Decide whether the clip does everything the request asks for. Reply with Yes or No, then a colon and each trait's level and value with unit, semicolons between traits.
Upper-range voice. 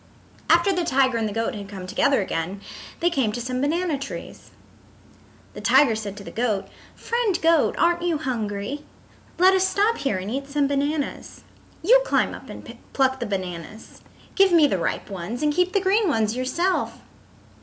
Yes: very high, 275 Hz